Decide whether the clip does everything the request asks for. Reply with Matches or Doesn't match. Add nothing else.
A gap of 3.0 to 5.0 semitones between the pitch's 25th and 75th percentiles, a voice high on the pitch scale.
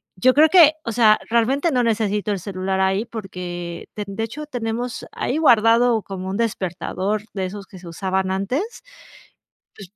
Matches